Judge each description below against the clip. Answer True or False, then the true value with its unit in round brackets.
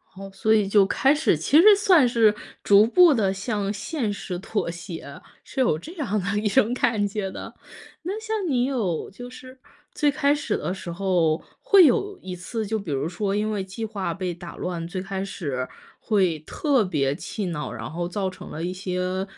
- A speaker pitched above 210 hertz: False (200 Hz)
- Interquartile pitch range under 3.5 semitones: False (5.3 semitones)